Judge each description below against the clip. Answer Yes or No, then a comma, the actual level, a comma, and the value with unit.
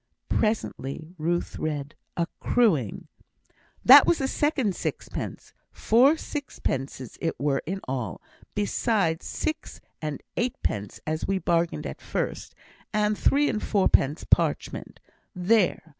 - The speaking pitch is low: No, medium, 180 Hz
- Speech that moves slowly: Yes, slow, 115 wpm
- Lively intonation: Yes, wide, 7.2 semitones